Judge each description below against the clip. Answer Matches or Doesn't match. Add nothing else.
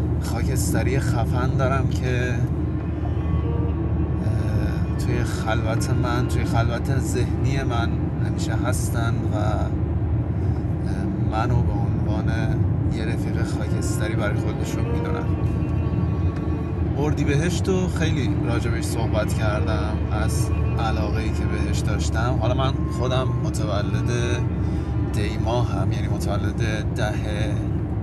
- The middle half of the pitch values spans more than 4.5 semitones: Doesn't match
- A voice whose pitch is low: Matches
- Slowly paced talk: Matches